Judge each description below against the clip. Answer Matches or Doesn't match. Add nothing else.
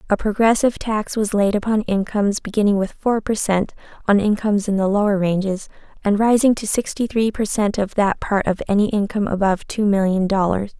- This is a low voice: Doesn't match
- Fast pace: Doesn't match